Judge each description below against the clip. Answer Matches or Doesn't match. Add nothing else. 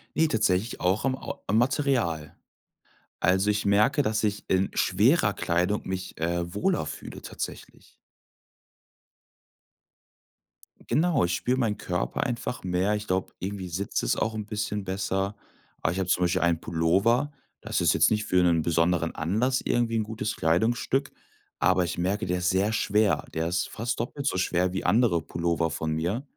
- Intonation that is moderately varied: Matches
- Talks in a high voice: Doesn't match